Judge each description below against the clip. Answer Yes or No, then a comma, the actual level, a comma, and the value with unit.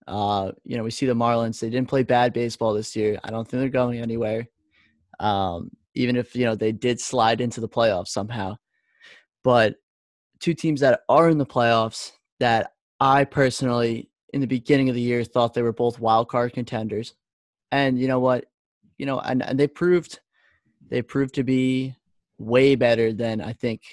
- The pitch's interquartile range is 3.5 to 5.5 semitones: No, average, 2.7 semitones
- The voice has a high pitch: No, low, 120 Hz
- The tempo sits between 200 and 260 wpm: No, average, 190 wpm